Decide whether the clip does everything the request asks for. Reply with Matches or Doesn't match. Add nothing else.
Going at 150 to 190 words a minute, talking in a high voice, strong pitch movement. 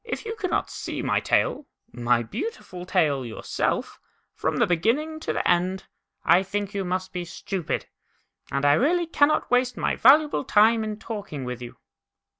Matches